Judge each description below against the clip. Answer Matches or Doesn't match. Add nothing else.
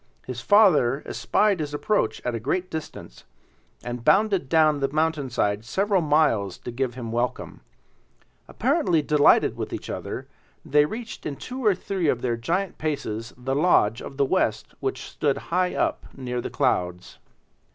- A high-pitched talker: Doesn't match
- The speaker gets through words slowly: Doesn't match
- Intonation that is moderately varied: Doesn't match